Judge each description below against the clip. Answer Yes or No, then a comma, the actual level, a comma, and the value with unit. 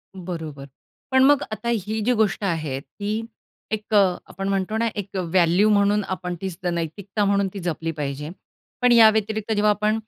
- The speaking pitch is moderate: No, high, 200 Hz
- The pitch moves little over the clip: No, average, 3.7 semitones